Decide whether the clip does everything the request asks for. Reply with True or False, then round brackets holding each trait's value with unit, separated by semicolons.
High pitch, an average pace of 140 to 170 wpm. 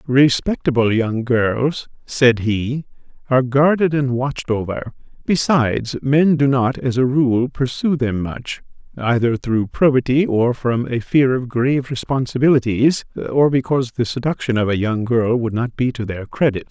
False (125 Hz; 160 wpm)